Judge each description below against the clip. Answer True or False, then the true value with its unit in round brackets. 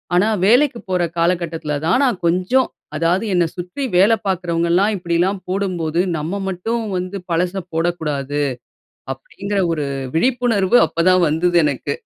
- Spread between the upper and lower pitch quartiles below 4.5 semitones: True (3.0 semitones)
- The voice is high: False (180 Hz)